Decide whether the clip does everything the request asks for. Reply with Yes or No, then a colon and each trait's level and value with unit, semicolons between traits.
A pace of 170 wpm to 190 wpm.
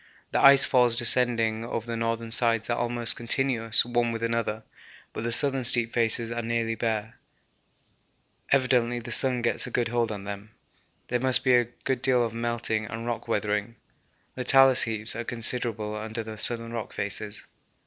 Yes: average, 175 wpm